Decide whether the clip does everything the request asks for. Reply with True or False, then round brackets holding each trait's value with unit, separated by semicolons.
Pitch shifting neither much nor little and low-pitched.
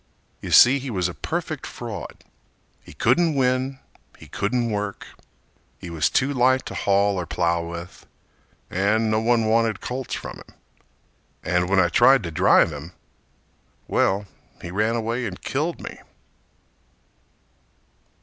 False (5.8 semitones; 110 Hz)